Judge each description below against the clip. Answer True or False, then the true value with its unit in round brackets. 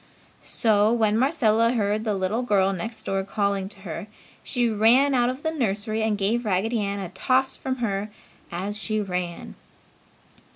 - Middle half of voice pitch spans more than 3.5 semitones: False (3.2 semitones)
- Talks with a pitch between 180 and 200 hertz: False (215 Hz)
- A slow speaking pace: False (165 wpm)